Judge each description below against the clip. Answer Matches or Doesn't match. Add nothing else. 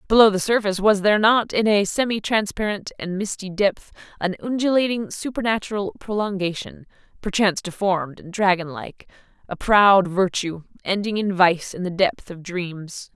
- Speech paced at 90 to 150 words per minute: Matches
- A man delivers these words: Doesn't match